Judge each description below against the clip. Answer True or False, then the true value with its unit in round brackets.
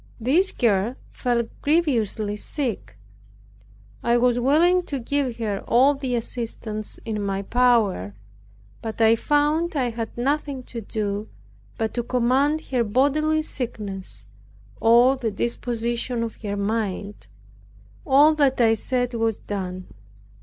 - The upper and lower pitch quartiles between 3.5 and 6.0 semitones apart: True (3.9 semitones)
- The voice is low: False (235 Hz)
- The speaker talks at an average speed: False (125 wpm)